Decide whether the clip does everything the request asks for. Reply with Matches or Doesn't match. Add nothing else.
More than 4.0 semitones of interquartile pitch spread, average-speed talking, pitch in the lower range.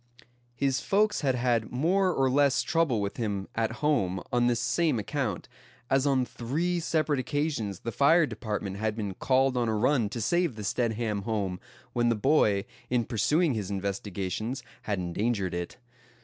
Matches